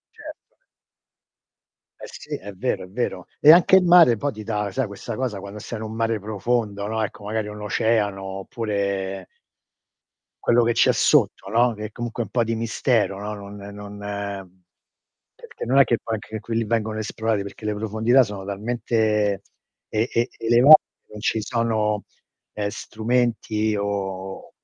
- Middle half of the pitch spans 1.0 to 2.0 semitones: No, narrow, 2.4 semitones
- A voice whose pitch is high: No, low, 110 Hz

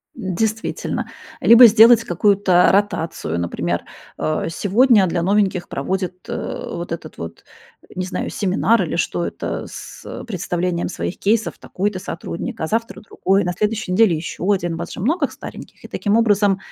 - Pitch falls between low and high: No, high, 195 Hz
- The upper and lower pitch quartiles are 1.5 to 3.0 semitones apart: No, average, 3.8 semitones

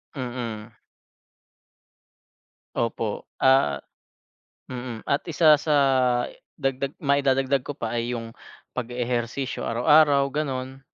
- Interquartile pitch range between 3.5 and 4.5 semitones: No, average, 2.8 semitones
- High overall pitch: No, low, 130 Hz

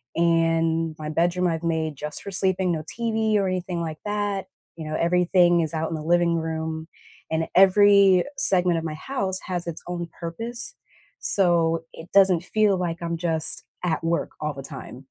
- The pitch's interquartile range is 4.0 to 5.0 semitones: No, narrow, 2.5 semitones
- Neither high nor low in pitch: Yes, medium, 170 Hz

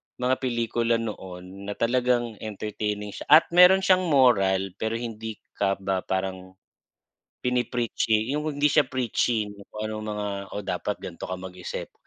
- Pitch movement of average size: Yes, average, 4.2 semitones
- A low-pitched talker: Yes, low, 110 Hz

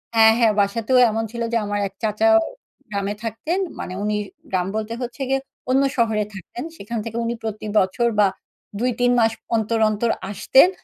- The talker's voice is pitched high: Yes, high, 225 Hz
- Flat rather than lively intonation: Yes, narrow, 2.3 semitones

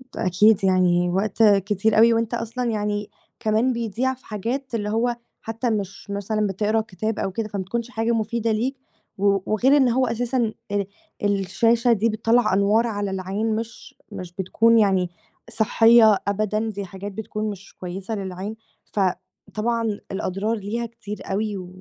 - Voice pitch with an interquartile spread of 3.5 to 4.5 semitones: No, narrow, 2.5 semitones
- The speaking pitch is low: No, high, 215 Hz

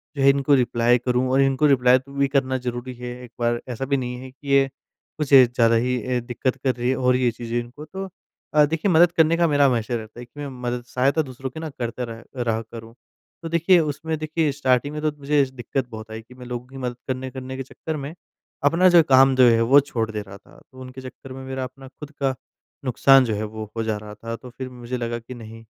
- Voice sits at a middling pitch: No, low, 130 Hz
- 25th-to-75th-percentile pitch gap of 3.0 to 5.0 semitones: No, narrow, 2.6 semitones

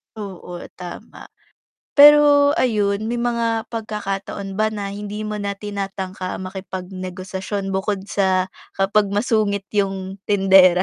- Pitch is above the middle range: Yes, high, 200 Hz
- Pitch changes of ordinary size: No, narrow, 2.0 semitones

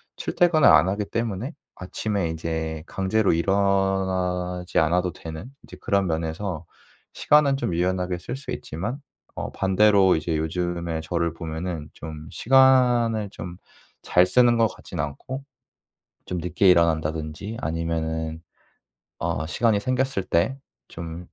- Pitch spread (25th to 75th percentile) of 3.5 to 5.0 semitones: Yes, average, 4.5 semitones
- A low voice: Yes, very low, 90 Hz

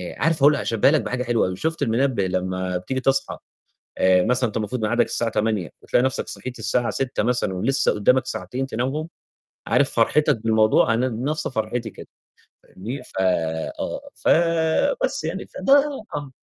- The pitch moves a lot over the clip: No, average, 4.2 semitones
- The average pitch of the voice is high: No, low, 120 Hz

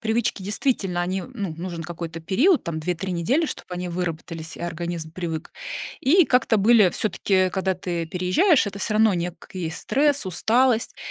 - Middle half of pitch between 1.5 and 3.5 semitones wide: No, average, 4.5 semitones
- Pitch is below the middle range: No, medium, 185 Hz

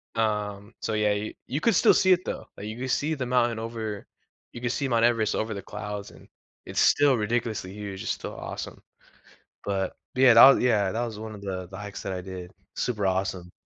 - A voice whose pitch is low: Yes, low, 110 Hz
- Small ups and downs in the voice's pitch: No, average, 3.1 semitones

